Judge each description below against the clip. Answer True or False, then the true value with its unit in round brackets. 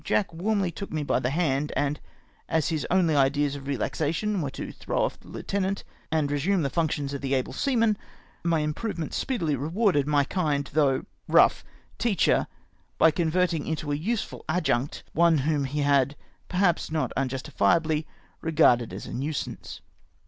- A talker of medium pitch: True (155 Hz)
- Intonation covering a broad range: False (3.8 semitones)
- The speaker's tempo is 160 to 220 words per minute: True (165 wpm)